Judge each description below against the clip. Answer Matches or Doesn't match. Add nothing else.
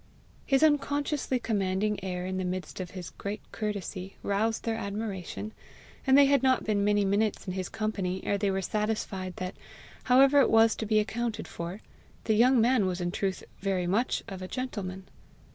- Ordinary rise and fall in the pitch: Matches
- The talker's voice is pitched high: Matches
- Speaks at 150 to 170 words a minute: Doesn't match